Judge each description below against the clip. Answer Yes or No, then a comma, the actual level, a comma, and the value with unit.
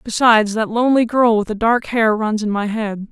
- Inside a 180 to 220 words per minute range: No, fast, 230 wpm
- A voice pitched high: Yes, high, 220 Hz